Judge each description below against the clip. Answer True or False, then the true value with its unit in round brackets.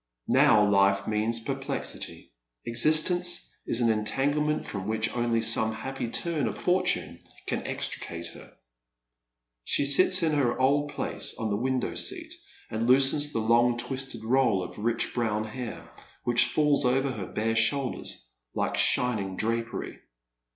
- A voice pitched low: True (120 Hz)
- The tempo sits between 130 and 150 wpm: True (140 wpm)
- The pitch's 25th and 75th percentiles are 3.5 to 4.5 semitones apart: True (3.8 semitones)